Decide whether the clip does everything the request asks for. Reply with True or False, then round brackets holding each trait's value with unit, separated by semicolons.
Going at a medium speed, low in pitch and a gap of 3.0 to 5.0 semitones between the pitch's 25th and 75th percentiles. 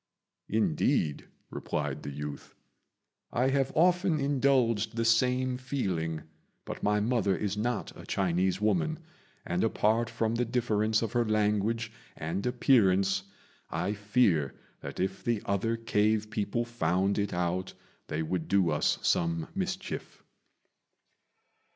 False (125 wpm; 105 Hz; 4.0 semitones)